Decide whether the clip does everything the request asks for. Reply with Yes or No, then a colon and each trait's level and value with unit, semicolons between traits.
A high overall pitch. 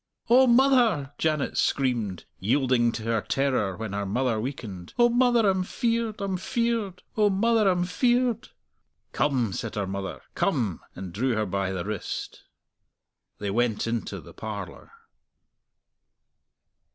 No: low, 135 Hz